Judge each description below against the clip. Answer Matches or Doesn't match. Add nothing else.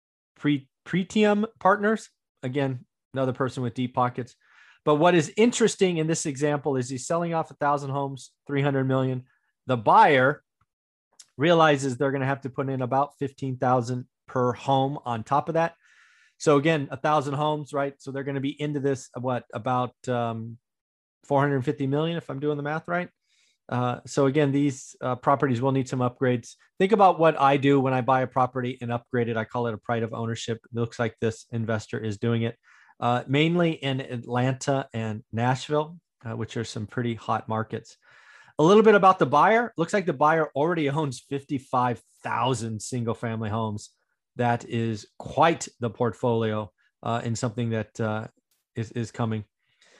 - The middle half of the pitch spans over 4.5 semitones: Doesn't match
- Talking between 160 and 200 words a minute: Matches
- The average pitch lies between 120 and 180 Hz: Matches